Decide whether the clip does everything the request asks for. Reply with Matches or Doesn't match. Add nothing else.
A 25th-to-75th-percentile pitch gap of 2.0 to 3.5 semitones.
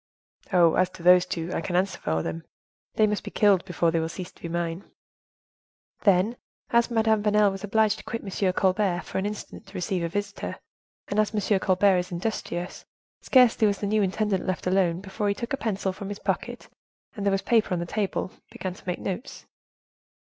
Matches